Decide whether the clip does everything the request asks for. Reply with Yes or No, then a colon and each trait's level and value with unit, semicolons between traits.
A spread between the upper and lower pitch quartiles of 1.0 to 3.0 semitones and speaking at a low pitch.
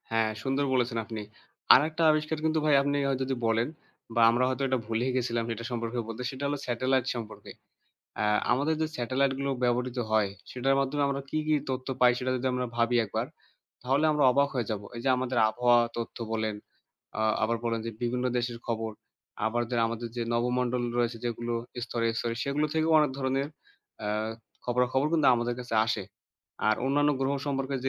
Yes: narrow, 2.6 semitones; low, 125 Hz